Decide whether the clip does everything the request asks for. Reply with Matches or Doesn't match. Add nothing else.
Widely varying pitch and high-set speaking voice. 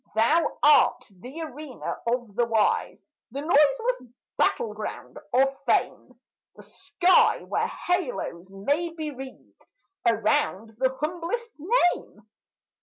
Matches